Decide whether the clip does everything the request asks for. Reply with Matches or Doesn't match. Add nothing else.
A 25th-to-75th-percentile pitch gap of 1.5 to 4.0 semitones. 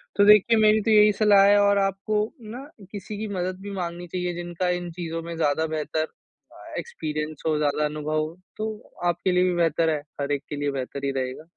Doesn't match